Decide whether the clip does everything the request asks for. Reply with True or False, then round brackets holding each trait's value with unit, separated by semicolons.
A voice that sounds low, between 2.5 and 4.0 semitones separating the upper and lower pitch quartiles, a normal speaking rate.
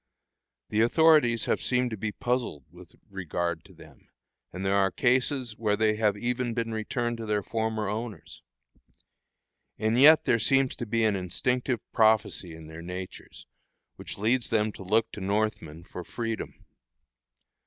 True (110 Hz; 3.4 semitones; 155 wpm)